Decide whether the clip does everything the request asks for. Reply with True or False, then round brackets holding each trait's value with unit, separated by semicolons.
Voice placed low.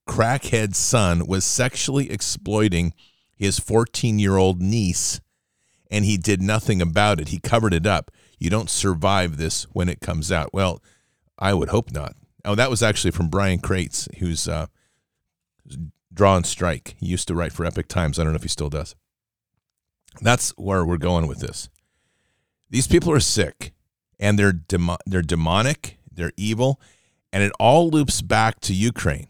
True (95 Hz)